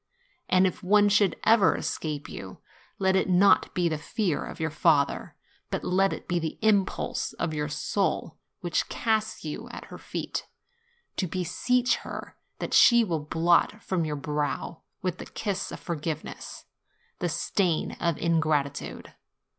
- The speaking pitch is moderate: Yes, medium, 175 Hz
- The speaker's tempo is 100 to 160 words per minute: Yes, average, 155 wpm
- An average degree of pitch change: Yes, average, 3.7 semitones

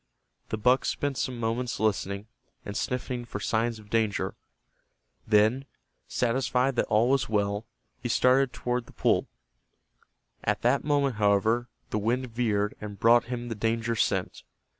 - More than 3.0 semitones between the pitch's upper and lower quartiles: No, average, 2.7 semitones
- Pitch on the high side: No, low, 115 Hz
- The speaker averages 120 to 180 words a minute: Yes, average, 145 wpm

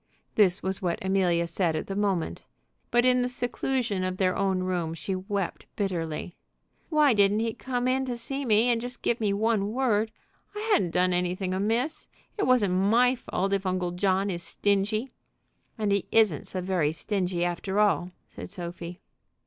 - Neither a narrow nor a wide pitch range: Yes, average, 4.1 semitones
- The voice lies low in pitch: No, high, 195 Hz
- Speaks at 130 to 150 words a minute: No, average, 175 wpm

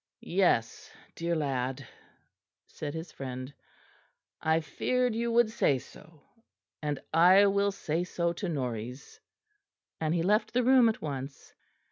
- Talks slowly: Yes, slow, 130 wpm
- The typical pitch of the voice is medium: Yes, medium, 160 Hz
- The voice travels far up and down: Yes, wide, 6.5 semitones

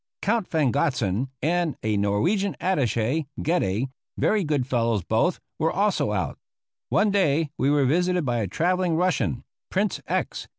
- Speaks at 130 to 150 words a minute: Yes, average, 145 wpm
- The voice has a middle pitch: Yes, medium, 145 Hz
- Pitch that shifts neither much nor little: No, wide, 7.6 semitones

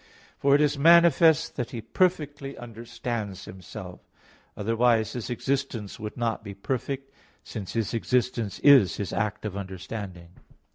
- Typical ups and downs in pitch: Yes, average, 4.8 semitones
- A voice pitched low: Yes, low, 115 Hz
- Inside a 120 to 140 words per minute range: Yes, slow, 135 wpm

